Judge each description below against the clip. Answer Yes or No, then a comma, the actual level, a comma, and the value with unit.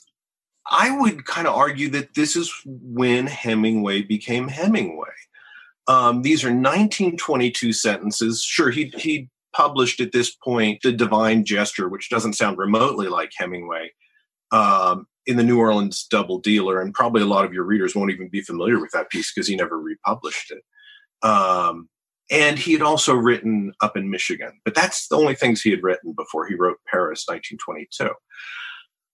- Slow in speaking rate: No, average, 165 wpm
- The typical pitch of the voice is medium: No, low, 120 Hz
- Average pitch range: No, wide, 5.8 semitones